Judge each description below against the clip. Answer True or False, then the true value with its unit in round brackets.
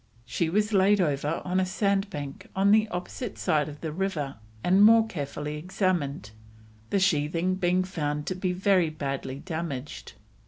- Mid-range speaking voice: True (180 Hz)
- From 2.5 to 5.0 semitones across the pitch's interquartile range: True (4.5 semitones)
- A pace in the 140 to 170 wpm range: True (155 wpm)